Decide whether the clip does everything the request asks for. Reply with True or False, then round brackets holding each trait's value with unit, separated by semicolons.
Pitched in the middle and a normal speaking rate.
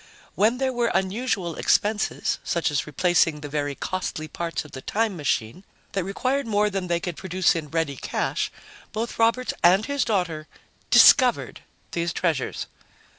True (180 Hz; 155 wpm)